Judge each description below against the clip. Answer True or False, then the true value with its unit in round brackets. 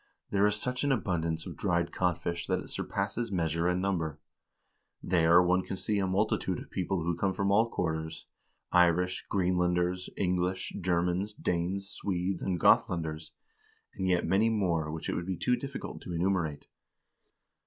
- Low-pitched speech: True (90 Hz)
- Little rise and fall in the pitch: True (2.3 semitones)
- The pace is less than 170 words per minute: True (160 wpm)